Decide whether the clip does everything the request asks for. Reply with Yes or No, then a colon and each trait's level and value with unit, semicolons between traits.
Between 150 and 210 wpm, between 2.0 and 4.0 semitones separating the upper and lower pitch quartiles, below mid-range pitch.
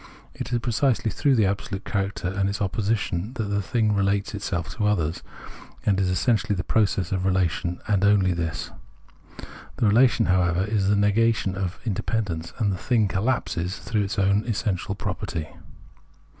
Yes: average, 165 wpm; average, 2.7 semitones; low, 100 Hz